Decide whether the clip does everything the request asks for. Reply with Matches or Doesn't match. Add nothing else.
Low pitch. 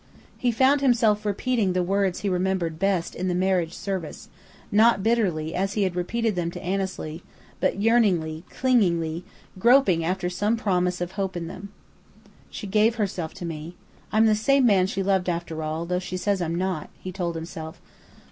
Doesn't match